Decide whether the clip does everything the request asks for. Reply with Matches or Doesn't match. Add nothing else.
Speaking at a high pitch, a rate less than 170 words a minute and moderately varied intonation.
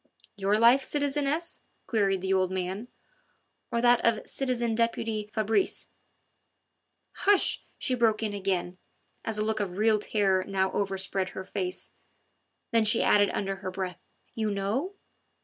Matches